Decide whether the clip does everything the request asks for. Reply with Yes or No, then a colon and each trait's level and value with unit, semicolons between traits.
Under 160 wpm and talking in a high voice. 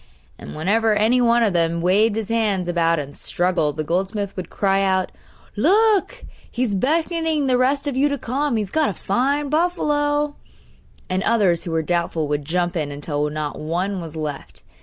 No: average, 180 wpm; high, 200 Hz